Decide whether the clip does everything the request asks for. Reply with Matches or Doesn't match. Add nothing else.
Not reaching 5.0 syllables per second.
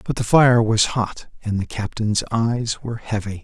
Matches